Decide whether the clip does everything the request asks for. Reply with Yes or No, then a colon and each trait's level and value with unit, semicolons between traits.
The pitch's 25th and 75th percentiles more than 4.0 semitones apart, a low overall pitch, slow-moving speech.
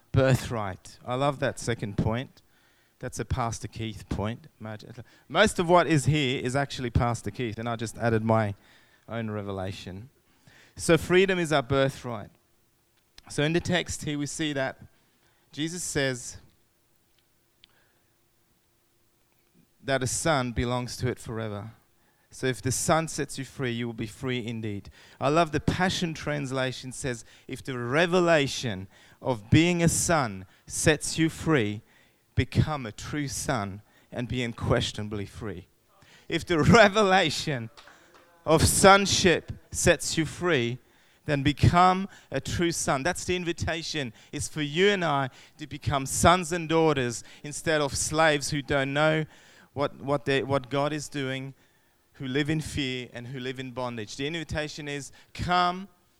No: average, 4.7 semitones; low, 130 Hz; average, 145 wpm